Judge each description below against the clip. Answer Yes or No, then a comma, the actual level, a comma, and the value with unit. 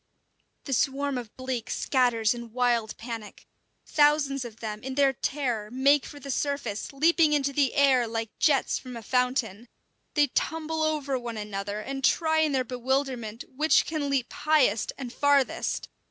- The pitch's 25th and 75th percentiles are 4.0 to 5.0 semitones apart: No, average, 3.5 semitones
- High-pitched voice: Yes, very high, 260 Hz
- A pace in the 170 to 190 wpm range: No, average, 160 wpm